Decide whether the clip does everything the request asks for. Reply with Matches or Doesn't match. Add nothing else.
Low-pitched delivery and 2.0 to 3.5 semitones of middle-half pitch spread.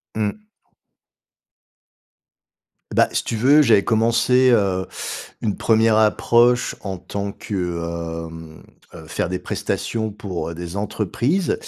Doesn't match